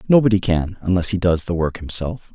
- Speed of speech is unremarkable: Yes, average, 180 wpm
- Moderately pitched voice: No, very low, 95 Hz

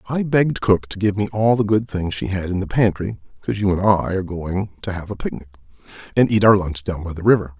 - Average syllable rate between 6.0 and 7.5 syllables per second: Yes, 6.2 syllables/s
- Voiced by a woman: No, male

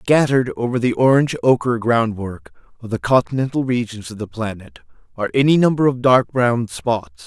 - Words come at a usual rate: Yes, average, 165 wpm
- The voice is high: No, low, 115 Hz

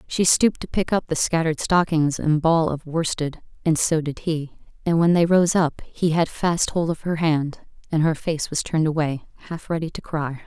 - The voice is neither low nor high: Yes, medium, 160 Hz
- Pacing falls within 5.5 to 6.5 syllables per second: No, 5.0 syllables/s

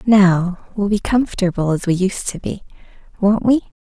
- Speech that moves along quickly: No, average, 170 wpm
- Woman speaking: Yes, female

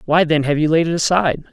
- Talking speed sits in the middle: No, fast, 275 wpm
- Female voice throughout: No, male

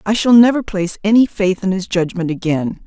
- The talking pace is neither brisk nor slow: No, fast, 210 wpm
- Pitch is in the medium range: No, high, 195 Hz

